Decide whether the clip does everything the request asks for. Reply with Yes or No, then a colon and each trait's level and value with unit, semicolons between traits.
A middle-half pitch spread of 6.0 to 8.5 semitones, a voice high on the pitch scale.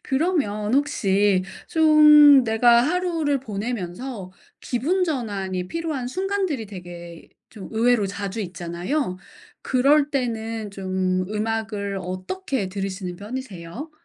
Yes: wide, 6.9 semitones; high, 225 Hz